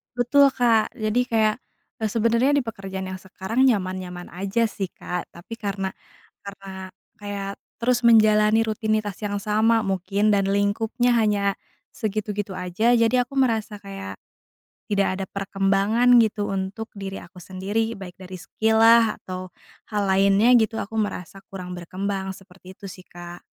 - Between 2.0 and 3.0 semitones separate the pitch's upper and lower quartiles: Yes, average, 2.7 semitones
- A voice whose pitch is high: Yes, high, 205 Hz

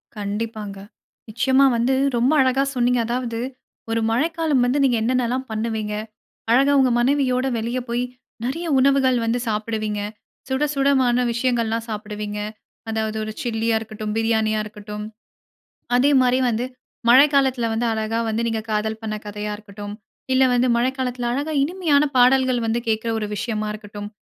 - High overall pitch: Yes, high, 235 Hz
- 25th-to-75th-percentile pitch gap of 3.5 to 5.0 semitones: No, average, 3.0 semitones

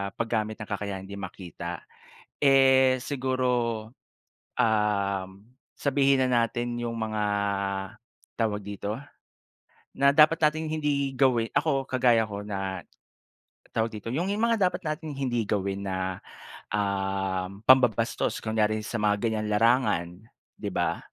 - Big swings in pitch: No, average, 4.7 semitones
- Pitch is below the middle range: Yes, low, 115 Hz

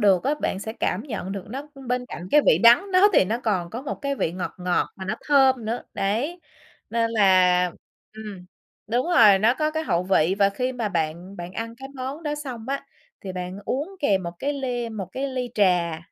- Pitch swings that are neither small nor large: No, wide, 6.0 semitones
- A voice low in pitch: No, high, 225 Hz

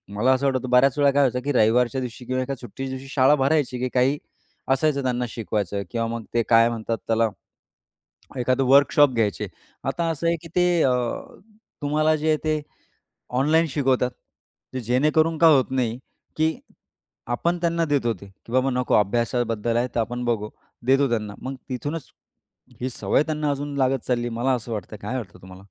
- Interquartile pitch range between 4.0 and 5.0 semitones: No, average, 3.5 semitones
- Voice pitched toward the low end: Yes, low, 130 Hz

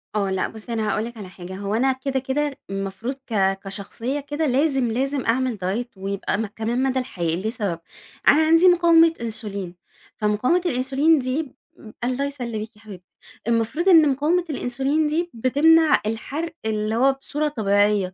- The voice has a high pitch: Yes, high, 245 Hz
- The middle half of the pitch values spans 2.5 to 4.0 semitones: No, wide, 5.4 semitones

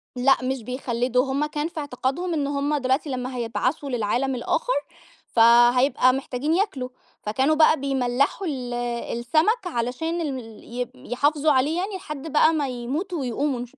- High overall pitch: Yes, very high, 270 Hz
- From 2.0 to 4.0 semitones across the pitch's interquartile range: Yes, average, 3.6 semitones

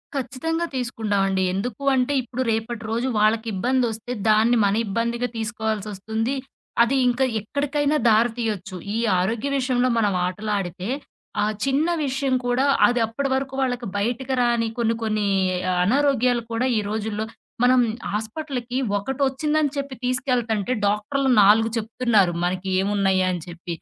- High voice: Yes, high, 230 Hz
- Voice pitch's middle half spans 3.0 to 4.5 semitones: Yes, average, 3.5 semitones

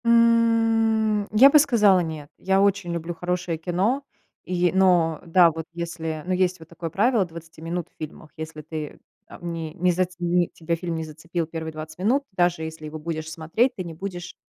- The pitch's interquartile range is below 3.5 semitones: Yes, average, 3.1 semitones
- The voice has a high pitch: No, medium, 175 Hz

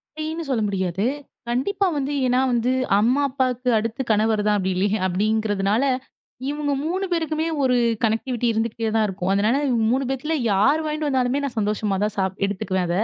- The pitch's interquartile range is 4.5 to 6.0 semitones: Yes, average, 4.9 semitones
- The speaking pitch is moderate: No, high, 230 Hz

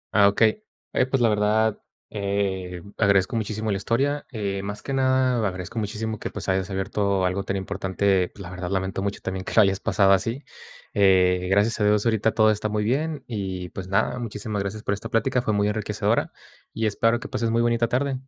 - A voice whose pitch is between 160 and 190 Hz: No, low, 105 Hz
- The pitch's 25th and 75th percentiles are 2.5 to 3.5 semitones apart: Yes, average, 2.8 semitones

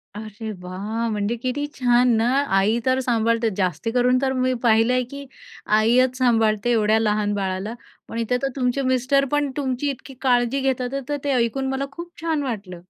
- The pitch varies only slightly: No, average, 3.2 semitones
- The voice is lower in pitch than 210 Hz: No, high, 245 Hz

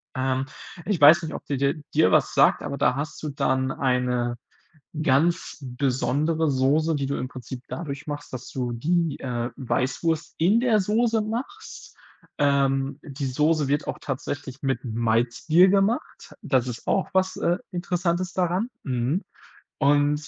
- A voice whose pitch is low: No, medium, 145 Hz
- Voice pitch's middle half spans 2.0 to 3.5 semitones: No, average, 4.5 semitones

